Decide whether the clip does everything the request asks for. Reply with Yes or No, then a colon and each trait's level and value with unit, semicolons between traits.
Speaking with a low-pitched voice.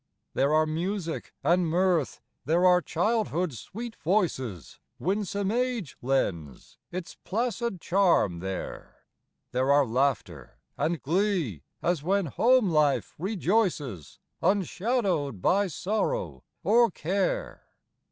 No: medium, 180 Hz